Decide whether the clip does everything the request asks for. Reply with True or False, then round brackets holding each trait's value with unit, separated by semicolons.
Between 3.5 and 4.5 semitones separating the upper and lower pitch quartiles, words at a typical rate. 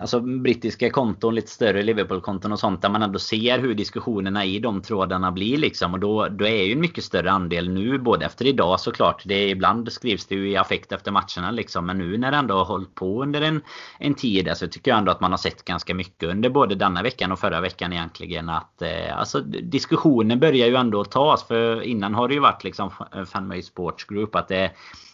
False (3.8 semitones; 220 wpm)